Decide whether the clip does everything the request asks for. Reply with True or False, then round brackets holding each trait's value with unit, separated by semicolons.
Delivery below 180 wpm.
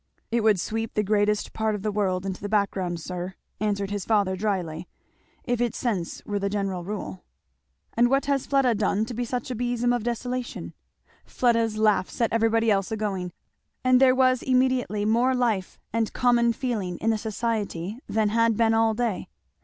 False (185 wpm)